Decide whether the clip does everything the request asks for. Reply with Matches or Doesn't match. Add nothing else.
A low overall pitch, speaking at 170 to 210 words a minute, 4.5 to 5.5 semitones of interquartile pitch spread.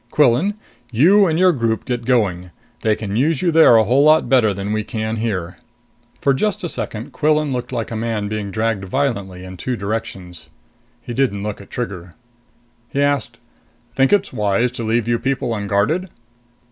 Matches